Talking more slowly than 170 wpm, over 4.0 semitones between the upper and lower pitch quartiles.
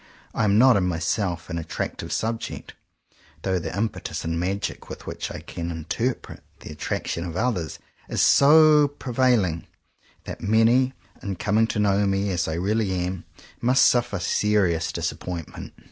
Yes: average, 160 wpm; average, 4.9 semitones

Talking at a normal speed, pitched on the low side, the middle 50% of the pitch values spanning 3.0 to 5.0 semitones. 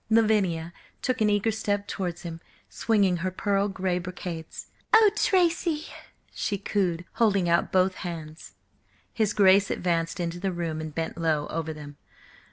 No: average, 150 wpm; medium, 185 Hz; average, 3.7 semitones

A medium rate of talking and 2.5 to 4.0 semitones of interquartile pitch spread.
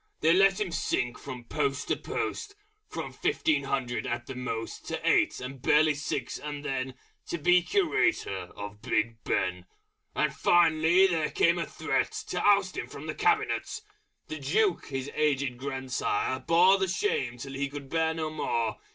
No: average, 170 wpm; average, 5.3 semitones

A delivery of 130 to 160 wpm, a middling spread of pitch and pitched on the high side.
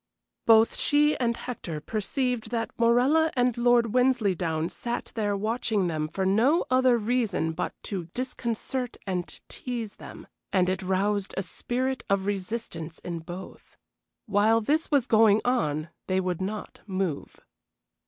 Yes: average, 140 wpm; average, 4.7 semitones; high, 215 Hz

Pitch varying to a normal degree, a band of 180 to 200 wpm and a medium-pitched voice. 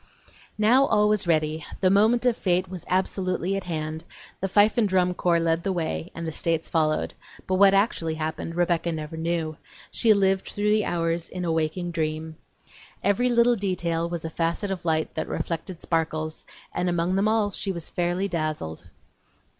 Yes: average, 3.3 semitones; average, 185 wpm; medium, 175 Hz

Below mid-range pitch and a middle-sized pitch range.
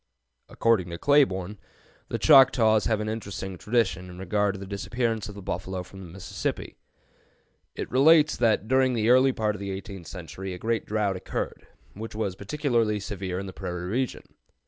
Yes: low, 105 Hz; average, 3.4 semitones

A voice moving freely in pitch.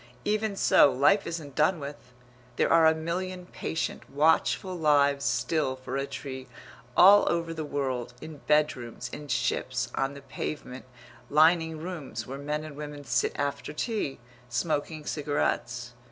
No: average, 3.1 semitones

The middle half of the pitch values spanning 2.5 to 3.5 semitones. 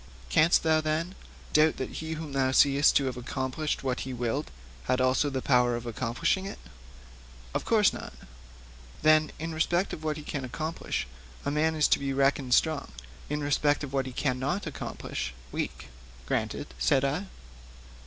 Yes: average, 3.2 semitones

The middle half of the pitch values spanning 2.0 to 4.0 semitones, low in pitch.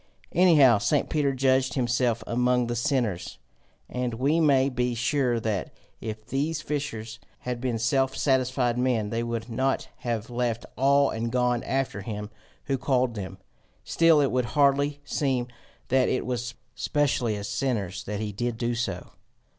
Yes: average, 2.8 semitones; low, 125 Hz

